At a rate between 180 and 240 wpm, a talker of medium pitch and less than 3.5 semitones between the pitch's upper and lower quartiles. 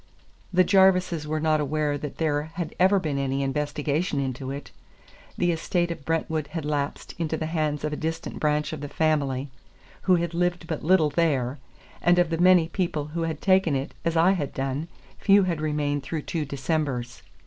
Yes: average, 190 wpm; medium, 155 Hz; average, 2.8 semitones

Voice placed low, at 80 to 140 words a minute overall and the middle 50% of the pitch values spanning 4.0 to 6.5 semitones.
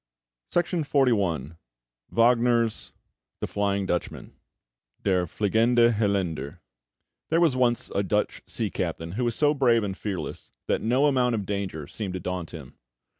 Yes: low, 105 Hz; slow, 135 wpm; average, 4.8 semitones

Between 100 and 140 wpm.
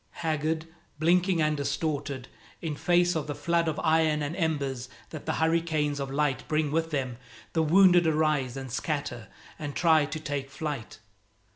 No: average, 160 wpm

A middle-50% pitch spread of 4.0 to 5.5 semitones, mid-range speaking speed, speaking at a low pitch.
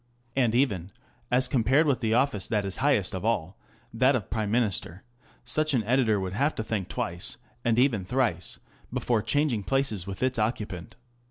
Yes: average, 4.5 semitones; average, 180 wpm; low, 115 Hz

